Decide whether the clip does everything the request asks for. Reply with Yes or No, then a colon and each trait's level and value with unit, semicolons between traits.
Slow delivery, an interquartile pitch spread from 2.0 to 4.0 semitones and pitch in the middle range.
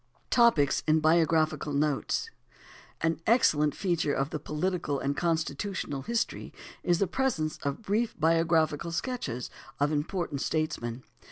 Yes: slow, 120 wpm; average, 3.6 semitones; medium, 160 Hz